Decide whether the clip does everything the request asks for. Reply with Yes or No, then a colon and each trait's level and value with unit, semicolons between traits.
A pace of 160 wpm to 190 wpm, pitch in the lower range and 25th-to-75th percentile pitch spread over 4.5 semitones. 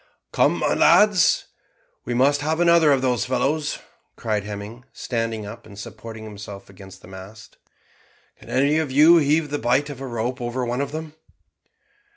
Yes: average, 170 wpm; low, 125 Hz; average, 5.0 semitones